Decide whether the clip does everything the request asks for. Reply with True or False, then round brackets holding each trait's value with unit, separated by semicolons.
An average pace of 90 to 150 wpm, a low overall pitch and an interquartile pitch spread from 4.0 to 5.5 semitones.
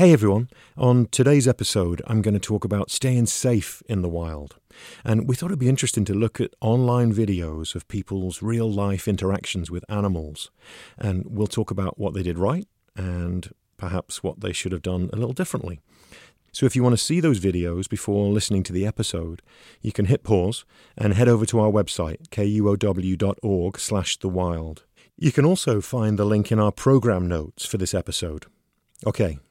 False (185 wpm; 105 Hz; 4.3 semitones)